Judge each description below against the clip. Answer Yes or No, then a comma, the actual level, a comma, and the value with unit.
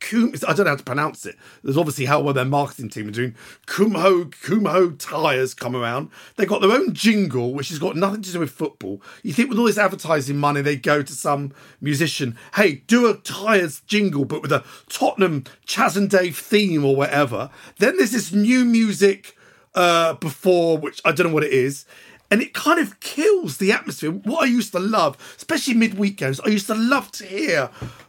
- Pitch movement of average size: No, wide, 6.5 semitones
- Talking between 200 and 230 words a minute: Yes, fast, 205 wpm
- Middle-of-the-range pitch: Yes, medium, 175 Hz